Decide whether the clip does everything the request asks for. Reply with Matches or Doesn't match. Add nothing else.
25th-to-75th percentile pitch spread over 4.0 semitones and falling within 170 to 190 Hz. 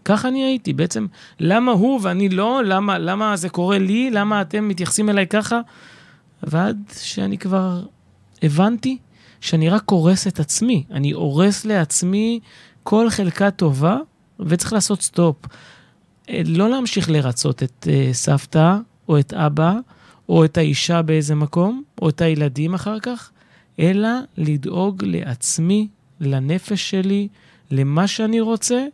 Matches